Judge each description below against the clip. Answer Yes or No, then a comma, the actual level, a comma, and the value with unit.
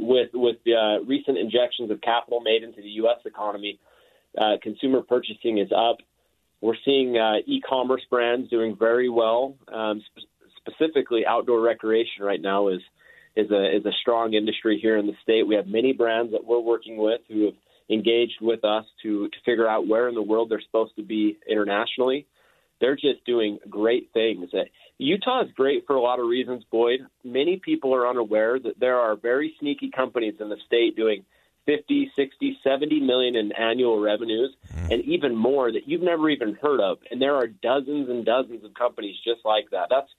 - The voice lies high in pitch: No, low, 115 Hz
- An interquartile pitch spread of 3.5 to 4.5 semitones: No, average, 3.1 semitones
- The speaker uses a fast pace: No, average, 190 wpm